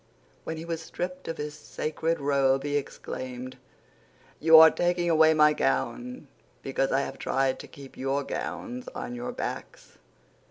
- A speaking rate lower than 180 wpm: Yes, average, 155 wpm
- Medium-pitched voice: Yes, medium, 160 Hz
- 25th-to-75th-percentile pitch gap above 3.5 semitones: Yes, average, 4.1 semitones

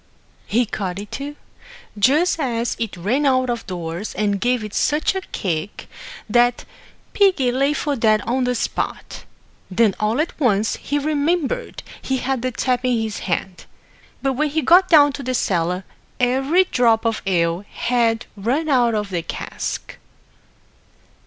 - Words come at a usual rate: Yes, average, 160 wpm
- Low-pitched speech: No, high, 245 Hz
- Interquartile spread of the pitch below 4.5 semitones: No, average, 5.0 semitones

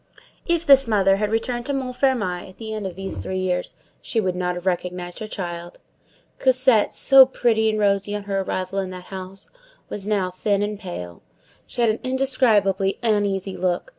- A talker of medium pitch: No, high, 200 Hz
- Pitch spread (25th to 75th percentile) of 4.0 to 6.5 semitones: No, average, 3.6 semitones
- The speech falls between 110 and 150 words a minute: No, average, 185 wpm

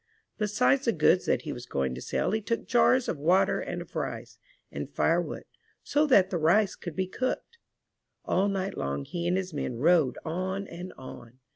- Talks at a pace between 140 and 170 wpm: No, average, 190 wpm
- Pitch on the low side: No, medium, 185 Hz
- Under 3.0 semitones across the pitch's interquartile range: No, average, 5.0 semitones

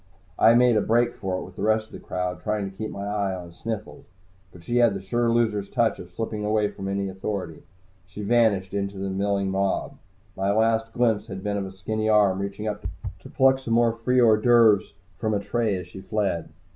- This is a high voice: No, low, 105 Hz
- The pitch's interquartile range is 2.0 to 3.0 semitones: Yes, narrow, 2.6 semitones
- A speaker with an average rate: No, fast, 220 wpm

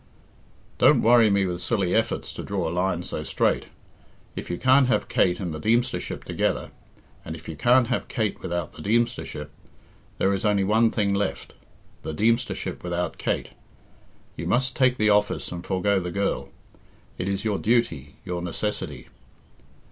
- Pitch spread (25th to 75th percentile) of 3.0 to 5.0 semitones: Yes, average, 4.4 semitones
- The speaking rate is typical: Yes, average, 165 wpm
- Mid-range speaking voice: No, low, 100 Hz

